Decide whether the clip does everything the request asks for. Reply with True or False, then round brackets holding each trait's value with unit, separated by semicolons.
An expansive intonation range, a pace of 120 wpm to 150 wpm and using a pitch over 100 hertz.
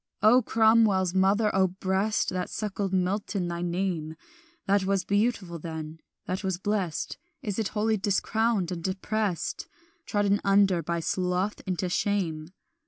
False (2.5 semitones; 135 wpm; 190 Hz)